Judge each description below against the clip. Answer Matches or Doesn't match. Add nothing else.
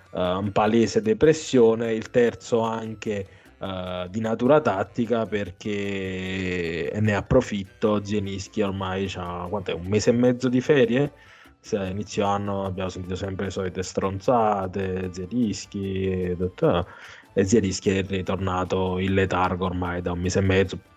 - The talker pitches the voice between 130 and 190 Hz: Doesn't match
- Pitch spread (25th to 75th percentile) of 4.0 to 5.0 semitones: Doesn't match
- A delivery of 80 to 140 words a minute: Matches